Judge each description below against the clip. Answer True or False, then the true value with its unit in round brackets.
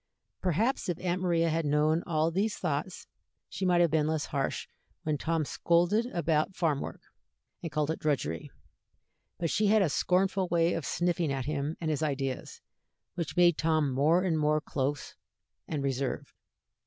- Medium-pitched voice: True (160 Hz)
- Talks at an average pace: True (165 wpm)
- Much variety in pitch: False (2.9 semitones)